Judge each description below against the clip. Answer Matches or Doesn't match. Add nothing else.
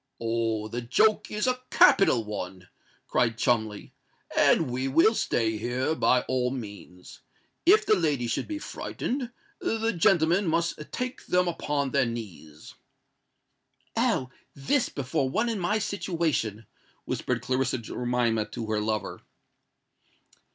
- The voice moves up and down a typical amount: Doesn't match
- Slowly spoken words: Matches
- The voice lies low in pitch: Matches